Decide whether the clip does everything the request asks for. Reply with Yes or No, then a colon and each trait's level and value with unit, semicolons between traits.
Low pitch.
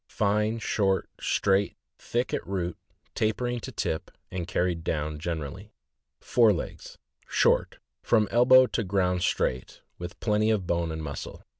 Yes: very low, 95 Hz